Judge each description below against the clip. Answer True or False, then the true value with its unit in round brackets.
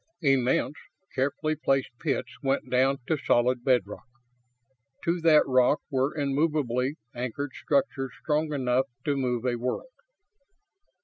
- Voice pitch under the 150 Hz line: True (135 Hz)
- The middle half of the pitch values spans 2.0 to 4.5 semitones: True (2.8 semitones)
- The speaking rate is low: True (120 wpm)